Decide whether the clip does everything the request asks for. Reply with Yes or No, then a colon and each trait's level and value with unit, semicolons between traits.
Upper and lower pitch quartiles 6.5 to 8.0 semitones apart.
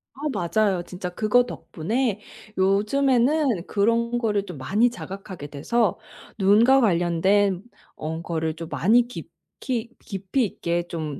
No: average, 5.2 semitones